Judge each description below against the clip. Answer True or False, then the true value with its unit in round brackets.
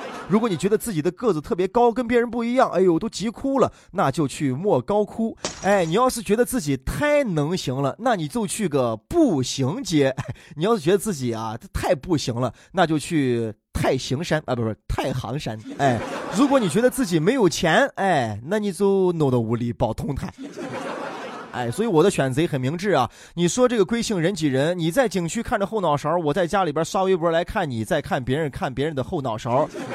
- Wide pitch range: True (7.8 semitones)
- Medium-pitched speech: True (175 Hz)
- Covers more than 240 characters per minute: True (300 characters per minute)